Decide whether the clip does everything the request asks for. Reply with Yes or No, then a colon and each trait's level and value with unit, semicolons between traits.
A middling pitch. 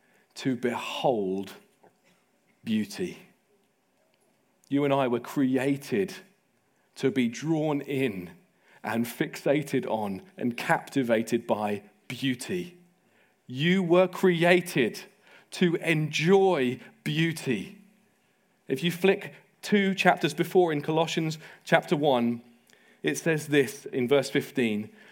Yes: medium, 155 Hz